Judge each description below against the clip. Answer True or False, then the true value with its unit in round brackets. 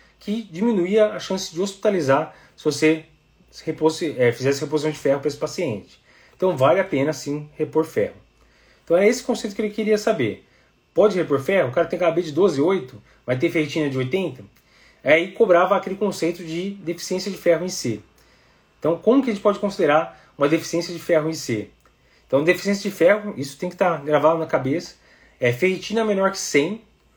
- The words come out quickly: True (195 wpm)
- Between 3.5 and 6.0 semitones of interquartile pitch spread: True (4.4 semitones)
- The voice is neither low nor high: True (170 Hz)